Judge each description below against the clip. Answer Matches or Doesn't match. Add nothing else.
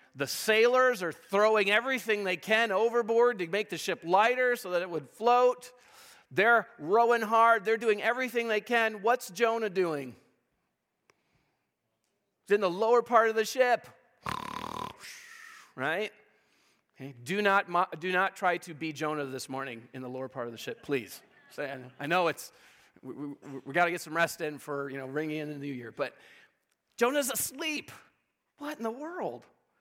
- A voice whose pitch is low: Doesn't match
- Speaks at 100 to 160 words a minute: Doesn't match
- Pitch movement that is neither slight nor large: Doesn't match